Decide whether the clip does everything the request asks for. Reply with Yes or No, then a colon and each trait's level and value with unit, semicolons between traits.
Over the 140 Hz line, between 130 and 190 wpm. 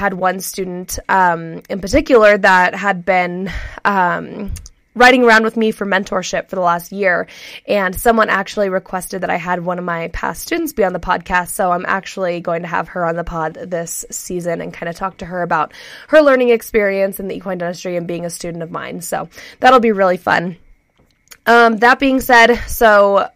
No: high, 190 Hz; average, 200 wpm